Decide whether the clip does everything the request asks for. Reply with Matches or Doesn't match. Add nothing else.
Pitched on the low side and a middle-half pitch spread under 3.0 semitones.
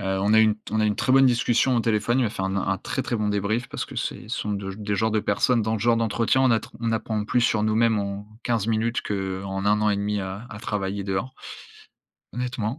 Matches